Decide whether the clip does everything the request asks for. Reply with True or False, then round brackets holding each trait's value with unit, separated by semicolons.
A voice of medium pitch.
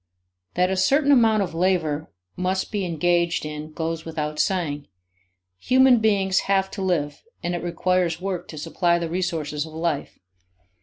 True (175 Hz)